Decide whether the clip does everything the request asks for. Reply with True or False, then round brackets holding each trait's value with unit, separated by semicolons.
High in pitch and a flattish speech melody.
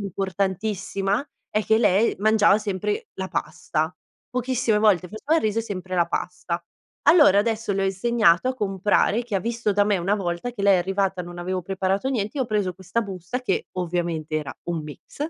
False (200 Hz; 3.1 semitones)